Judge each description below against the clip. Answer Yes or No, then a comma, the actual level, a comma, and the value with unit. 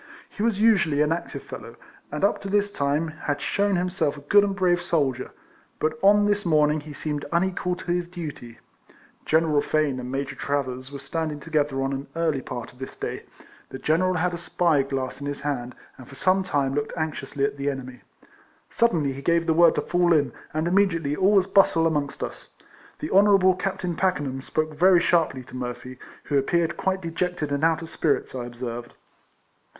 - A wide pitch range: No, average, 4.2 semitones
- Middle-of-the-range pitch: Yes, medium, 155 Hz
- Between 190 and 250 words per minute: Yes, average, 195 wpm